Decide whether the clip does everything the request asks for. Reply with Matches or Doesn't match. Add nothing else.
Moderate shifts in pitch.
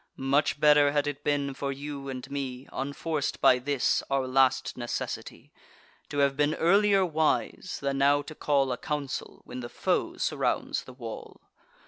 Doesn't match